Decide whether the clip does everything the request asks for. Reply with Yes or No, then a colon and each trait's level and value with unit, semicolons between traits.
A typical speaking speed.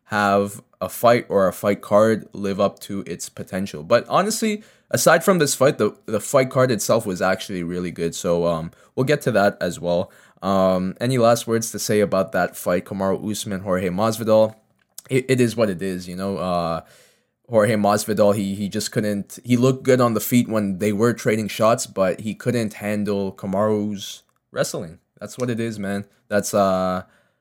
Yes: average, 190 wpm